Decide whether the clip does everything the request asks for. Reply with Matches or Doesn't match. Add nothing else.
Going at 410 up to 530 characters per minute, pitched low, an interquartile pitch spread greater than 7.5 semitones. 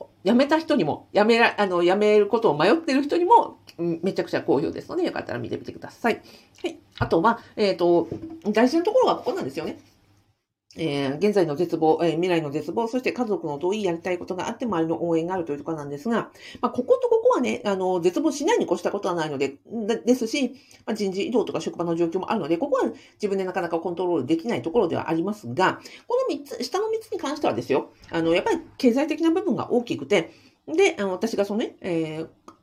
Doesn't match